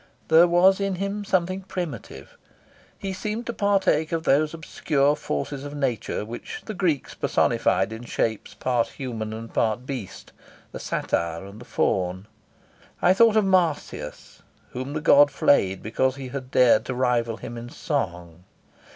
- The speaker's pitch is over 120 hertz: Yes, medium, 140 Hz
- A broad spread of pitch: Yes, wide, 7.5 semitones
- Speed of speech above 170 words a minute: No, average, 155 wpm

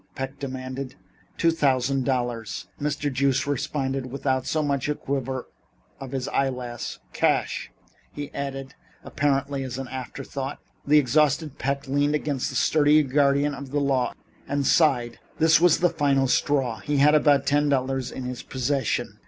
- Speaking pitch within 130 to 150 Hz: Yes, low, 135 Hz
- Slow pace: No, average, 155 wpm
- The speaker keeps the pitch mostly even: Yes, narrow, 1.8 semitones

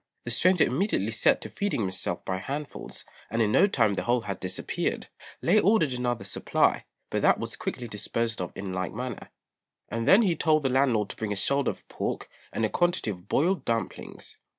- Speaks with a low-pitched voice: Yes, low, 115 Hz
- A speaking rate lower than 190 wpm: No, average, 195 wpm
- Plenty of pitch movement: Yes, wide, 6.5 semitones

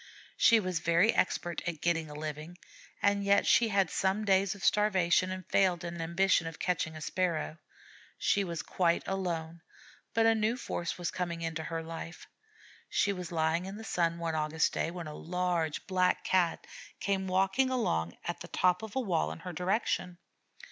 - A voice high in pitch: No, medium, 180 Hz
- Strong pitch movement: No, average, 2.7 semitones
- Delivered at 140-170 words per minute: No, average, 180 wpm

